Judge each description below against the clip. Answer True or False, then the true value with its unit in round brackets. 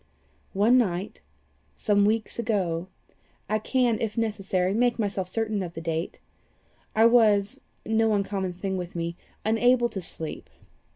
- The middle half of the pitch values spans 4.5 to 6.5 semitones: False (3.4 semitones)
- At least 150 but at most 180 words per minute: False (135 wpm)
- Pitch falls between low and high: False (205 Hz)